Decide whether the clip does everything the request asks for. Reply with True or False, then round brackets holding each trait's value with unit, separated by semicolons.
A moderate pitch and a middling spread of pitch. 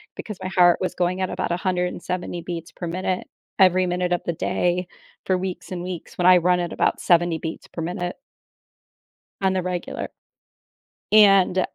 False (180 Hz; 1.0 semitones)